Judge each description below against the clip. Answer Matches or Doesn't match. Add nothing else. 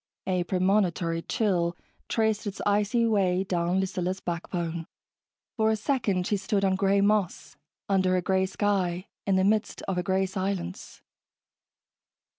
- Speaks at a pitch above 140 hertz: Matches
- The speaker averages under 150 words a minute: Matches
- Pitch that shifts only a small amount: Matches